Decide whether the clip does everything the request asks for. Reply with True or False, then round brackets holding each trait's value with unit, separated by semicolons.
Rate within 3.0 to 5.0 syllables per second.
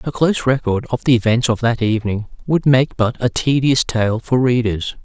False (5.2 syllables/s)